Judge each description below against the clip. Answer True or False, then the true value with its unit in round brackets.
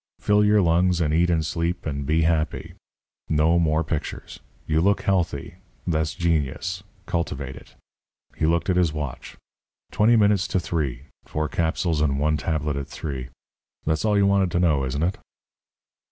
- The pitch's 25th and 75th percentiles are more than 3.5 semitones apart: False (2.9 semitones)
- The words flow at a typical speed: True (165 wpm)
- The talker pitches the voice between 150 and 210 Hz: False (80 Hz)